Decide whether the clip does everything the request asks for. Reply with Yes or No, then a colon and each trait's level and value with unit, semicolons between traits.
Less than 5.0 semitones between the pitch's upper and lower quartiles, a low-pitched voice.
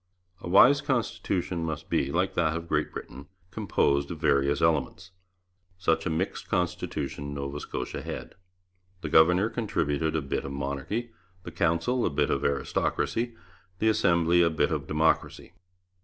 Yes: average, 4.2 semitones; very low, 85 Hz